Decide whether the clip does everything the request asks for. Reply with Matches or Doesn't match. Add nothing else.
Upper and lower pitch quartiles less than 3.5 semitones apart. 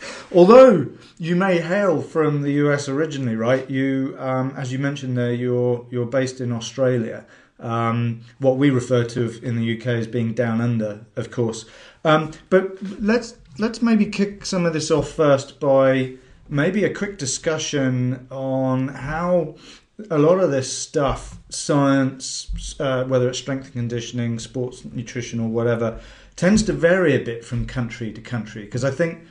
Doesn't match